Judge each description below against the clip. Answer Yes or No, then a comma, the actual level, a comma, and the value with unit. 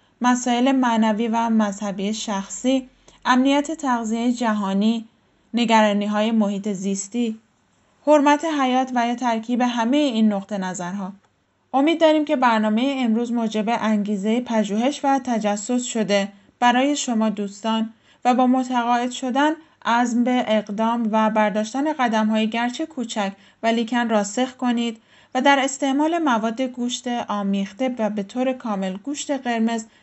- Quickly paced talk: No, average, 130 wpm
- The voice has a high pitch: Yes, high, 235 Hz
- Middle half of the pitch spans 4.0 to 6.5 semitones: No, average, 3.0 semitones